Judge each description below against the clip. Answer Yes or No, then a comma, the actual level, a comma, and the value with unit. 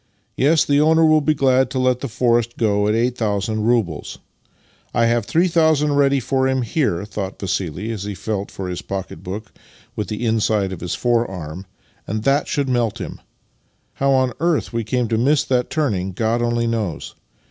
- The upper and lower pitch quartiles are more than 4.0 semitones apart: Yes, average, 4.5 semitones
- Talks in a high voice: No, low, 115 Hz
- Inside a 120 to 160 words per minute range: No, average, 190 wpm